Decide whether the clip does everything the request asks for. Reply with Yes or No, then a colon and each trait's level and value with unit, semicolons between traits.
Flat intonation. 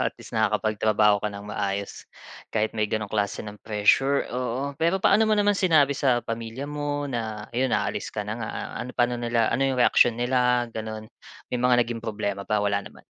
No: average, 3.7 semitones